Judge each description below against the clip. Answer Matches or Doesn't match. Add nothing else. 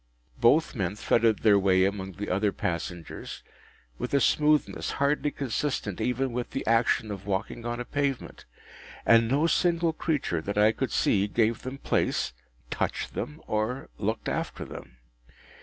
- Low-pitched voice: Matches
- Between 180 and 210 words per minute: Doesn't match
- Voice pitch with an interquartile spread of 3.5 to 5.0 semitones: Doesn't match